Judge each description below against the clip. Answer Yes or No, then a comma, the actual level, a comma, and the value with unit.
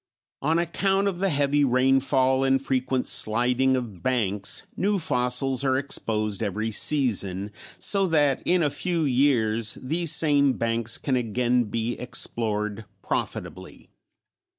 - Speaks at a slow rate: Yes, slow, 130 wpm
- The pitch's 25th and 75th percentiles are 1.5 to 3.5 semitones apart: No, average, 4.0 semitones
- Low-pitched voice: Yes, low, 130 Hz